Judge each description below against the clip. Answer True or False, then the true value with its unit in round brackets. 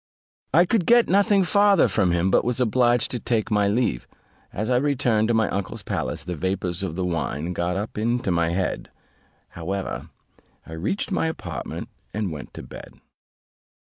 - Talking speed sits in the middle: True (175 wpm)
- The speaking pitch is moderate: False (105 Hz)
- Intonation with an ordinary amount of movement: False (6.0 semitones)